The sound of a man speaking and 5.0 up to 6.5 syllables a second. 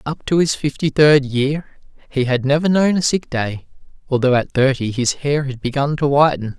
No: male; 4.8 syllables/s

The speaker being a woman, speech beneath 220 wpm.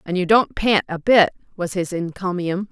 Yes: female; average, 200 wpm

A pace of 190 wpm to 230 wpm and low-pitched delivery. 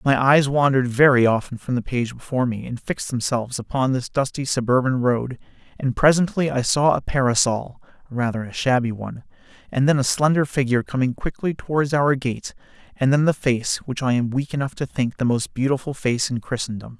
Yes: average, 195 wpm; low, 130 Hz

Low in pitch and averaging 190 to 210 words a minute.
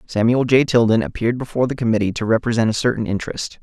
Yes: low, 115 Hz; average, 200 wpm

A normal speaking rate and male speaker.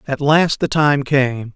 Yes: average, 190 wpm; male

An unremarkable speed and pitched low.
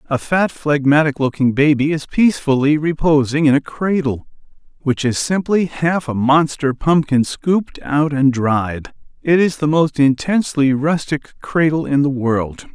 No: average, 150 wpm; medium, 145 Hz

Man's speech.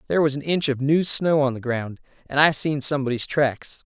Yes: male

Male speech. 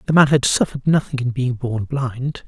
Yes: male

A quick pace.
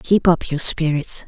No: average, 190 wpm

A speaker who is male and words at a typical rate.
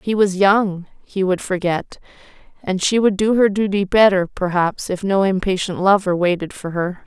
No: female; average, 180 wpm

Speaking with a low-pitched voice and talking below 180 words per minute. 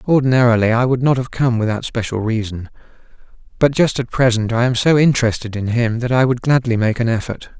No: low, 120 Hz; fast, 205 wpm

